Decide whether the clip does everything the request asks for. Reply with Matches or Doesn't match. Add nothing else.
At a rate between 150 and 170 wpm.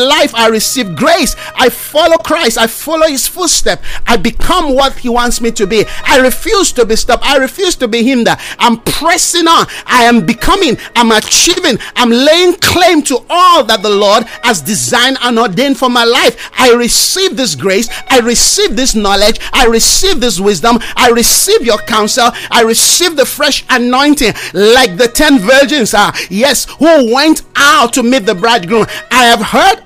Doesn't match